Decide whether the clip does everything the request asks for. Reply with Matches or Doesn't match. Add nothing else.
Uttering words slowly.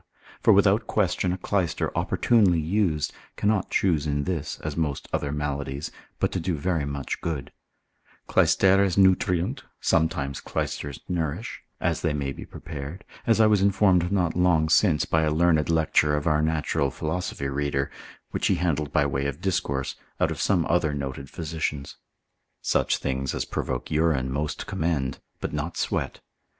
Doesn't match